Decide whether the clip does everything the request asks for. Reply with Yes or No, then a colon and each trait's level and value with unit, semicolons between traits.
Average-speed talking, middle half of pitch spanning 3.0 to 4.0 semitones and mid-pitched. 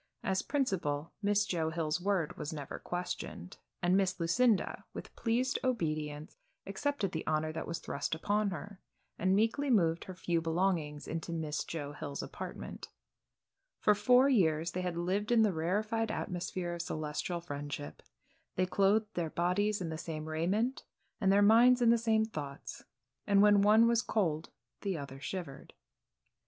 No: average, 160 wpm; average, 4.8 semitones; medium, 180 Hz